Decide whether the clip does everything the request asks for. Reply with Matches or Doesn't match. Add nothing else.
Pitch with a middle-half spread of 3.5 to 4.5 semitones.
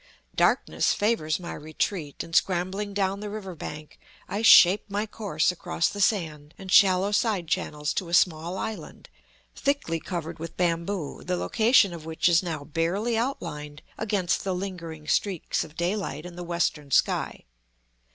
Matches